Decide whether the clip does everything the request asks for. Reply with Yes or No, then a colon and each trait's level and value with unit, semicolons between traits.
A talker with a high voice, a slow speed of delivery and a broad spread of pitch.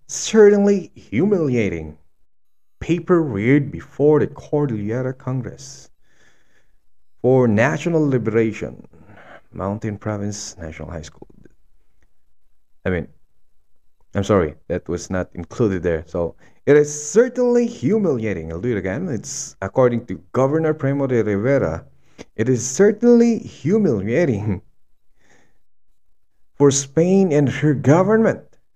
No: low, 115 Hz; slow, 105 wpm; wide, 8.5 semitones